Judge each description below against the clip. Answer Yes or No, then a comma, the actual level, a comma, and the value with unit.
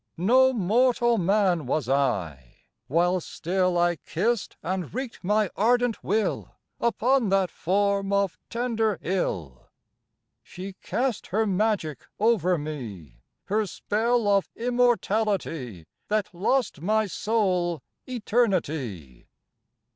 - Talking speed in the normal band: No, slow, 105 wpm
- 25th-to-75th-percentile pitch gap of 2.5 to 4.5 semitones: No, average, 5.1 semitones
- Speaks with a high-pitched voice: Yes, high, 195 Hz